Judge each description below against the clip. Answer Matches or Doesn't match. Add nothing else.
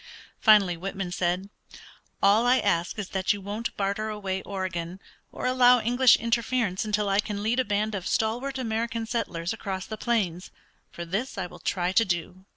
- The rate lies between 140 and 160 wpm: Doesn't match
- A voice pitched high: Matches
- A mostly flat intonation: Doesn't match